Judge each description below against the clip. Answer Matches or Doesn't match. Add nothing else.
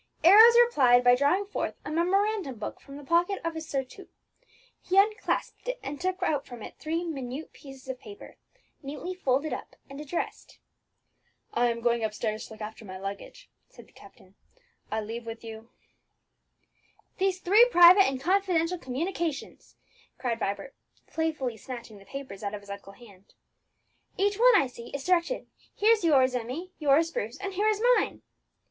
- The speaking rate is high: Doesn't match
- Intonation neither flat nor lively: Doesn't match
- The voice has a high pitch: Matches